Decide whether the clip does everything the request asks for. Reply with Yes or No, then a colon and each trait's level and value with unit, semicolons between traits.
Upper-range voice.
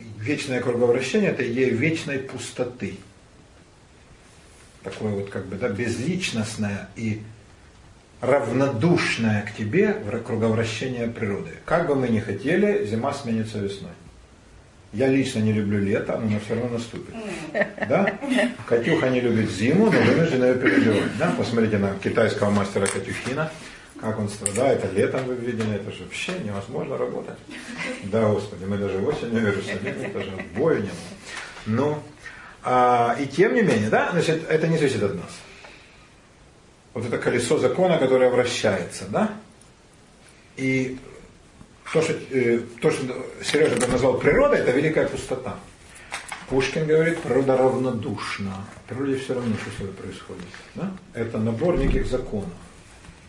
No: low, 115 Hz